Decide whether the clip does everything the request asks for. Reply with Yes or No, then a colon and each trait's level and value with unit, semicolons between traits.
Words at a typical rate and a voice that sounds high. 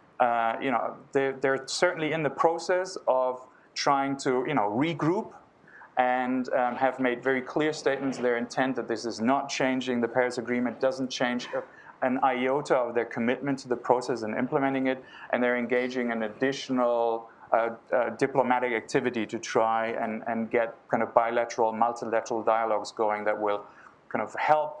No: average, 170 wpm; low, 125 Hz